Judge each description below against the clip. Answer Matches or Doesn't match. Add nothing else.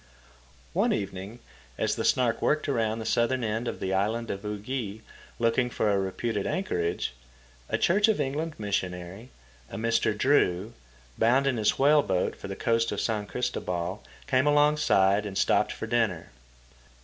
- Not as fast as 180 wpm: Matches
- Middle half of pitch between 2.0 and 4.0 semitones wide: Doesn't match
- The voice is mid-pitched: Doesn't match